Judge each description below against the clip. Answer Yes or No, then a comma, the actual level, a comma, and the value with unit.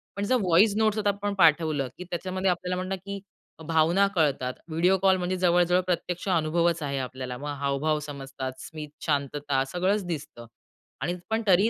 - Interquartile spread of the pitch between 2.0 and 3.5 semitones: No, average, 4.3 semitones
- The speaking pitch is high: No, medium, 170 Hz